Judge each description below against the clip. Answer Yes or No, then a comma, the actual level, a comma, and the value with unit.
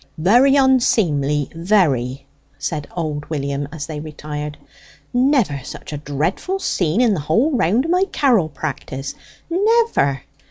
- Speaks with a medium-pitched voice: Yes, medium, 160 Hz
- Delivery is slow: Yes, slow, 130 wpm